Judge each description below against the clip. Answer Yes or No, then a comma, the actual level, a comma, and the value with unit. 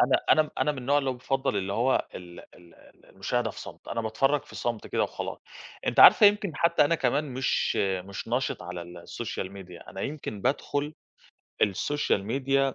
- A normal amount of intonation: No, wide, 6.4 semitones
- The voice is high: No, low, 125 Hz